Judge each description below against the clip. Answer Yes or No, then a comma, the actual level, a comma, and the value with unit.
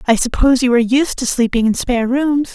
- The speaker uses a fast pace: Yes, fast, 235 wpm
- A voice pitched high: Yes, very high, 250 Hz